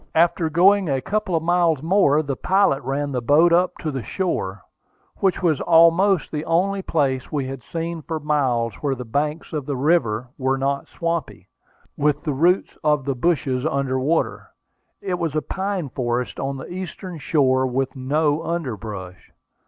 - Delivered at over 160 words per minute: Yes, average, 170 wpm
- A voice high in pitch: No, medium, 150 Hz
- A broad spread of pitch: No, average, 4.3 semitones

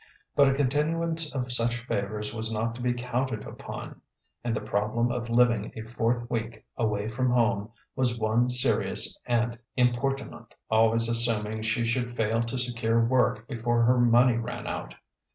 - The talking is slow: No, average, 160 wpm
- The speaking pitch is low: Yes, low, 120 Hz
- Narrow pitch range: Yes, narrow, 1.8 semitones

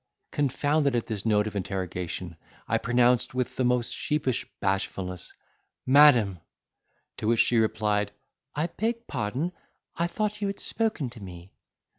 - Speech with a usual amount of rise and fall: No, wide, 6.1 semitones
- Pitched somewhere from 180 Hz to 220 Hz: No, low, 120 Hz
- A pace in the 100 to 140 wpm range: Yes, slow, 135 wpm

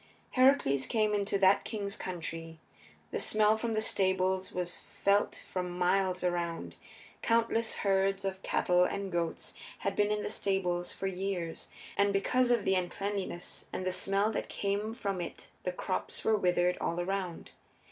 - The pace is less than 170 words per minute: Yes, average, 155 wpm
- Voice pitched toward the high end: Yes, high, 195 Hz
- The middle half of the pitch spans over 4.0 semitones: No, narrow, 2.4 semitones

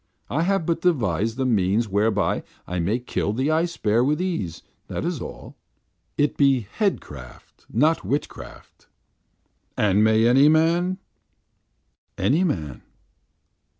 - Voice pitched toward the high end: No, low, 125 Hz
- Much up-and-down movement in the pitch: Yes, wide, 7.5 semitones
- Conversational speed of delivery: No, slow, 125 wpm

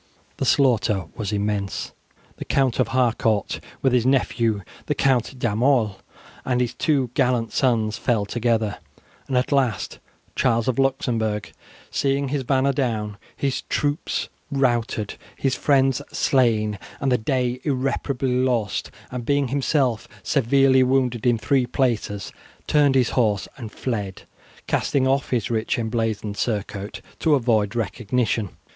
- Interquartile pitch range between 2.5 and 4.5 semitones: Yes, average, 3.5 semitones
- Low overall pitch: Yes, low, 125 Hz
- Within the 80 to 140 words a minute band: Yes, slow, 135 wpm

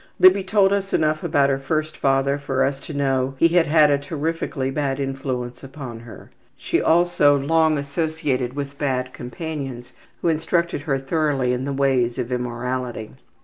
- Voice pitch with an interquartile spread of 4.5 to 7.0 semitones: No, average, 3.2 semitones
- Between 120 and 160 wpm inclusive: No, average, 170 wpm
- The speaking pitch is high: No, medium, 140 Hz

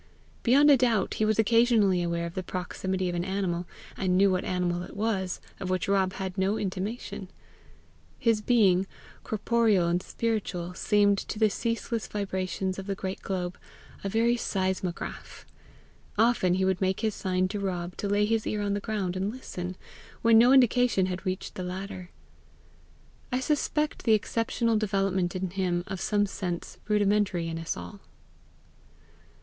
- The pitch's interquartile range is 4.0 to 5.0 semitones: No, average, 2.9 semitones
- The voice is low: No, high, 195 Hz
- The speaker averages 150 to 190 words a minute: Yes, average, 165 wpm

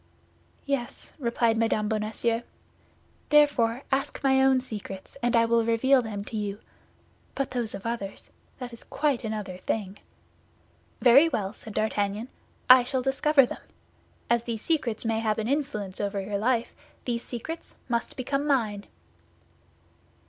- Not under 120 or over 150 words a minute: Yes, average, 140 wpm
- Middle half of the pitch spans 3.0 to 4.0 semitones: Yes, average, 3.5 semitones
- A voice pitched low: No, high, 235 Hz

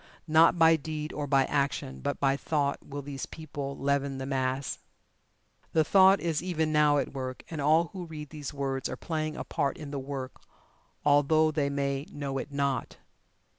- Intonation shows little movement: Yes, narrow, 2.1 semitones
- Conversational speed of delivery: Yes, average, 180 wpm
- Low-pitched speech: No, medium, 145 Hz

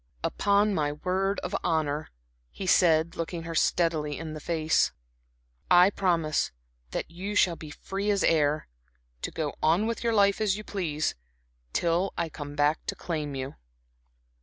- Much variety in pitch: No, average, 4.0 semitones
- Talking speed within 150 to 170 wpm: Yes, average, 160 wpm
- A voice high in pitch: No, medium, 165 Hz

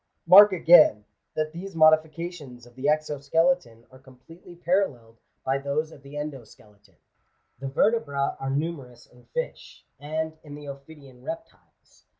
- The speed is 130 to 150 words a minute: Yes, average, 145 wpm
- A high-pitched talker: No, medium, 145 Hz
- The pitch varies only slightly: No, average, 3.9 semitones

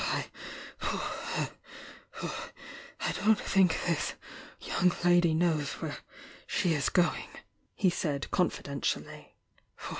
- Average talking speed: No, slow, 85 wpm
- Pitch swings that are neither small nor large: Yes, average, 3.0 semitones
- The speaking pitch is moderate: Yes, medium, 175 Hz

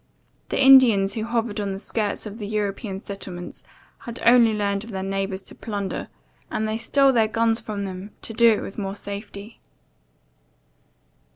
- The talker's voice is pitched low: No, high, 210 Hz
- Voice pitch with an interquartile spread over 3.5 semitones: No, narrow, 2.5 semitones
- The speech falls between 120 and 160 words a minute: No, average, 170 wpm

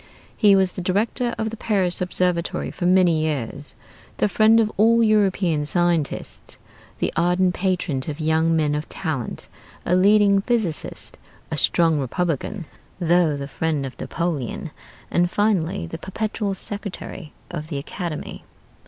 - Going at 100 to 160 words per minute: Yes, average, 140 wpm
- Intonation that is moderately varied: Yes, average, 4.0 semitones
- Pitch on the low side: No, medium, 175 Hz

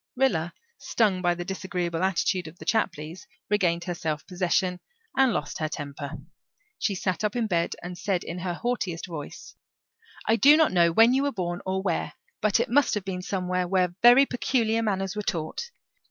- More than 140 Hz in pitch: Yes, medium, 185 Hz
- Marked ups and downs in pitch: No, average, 4.1 semitones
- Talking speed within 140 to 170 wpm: No, average, 185 wpm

